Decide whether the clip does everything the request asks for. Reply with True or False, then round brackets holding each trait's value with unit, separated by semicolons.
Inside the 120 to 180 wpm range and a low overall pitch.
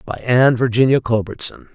True (140 wpm; 120 Hz)